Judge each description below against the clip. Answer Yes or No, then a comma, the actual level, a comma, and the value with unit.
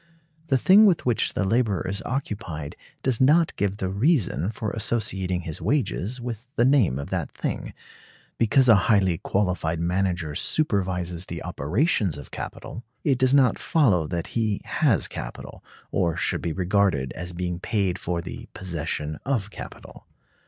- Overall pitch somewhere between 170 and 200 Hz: No, low, 100 Hz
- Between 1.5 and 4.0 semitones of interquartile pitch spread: No, wide, 5.6 semitones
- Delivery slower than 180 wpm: Yes, average, 155 wpm